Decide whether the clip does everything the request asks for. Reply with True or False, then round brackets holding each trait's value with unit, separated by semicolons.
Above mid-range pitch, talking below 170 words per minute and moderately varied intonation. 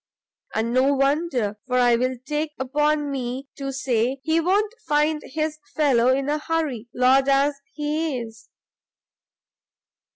True (275 Hz; 135 wpm; 3.1 semitones)